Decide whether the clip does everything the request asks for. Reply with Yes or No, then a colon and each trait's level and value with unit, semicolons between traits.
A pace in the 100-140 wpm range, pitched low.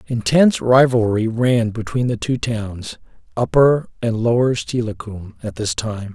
Yes: slow, 135 wpm; low, 115 Hz